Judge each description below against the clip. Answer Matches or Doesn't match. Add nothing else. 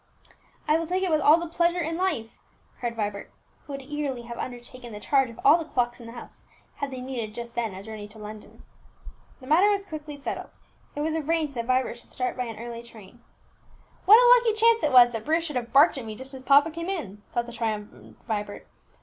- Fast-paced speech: Matches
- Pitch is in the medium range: Doesn't match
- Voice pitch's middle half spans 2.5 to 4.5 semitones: Doesn't match